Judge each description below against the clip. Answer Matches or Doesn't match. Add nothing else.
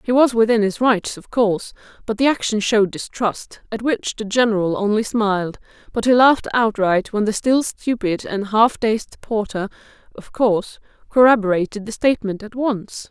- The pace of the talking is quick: Doesn't match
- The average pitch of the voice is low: Doesn't match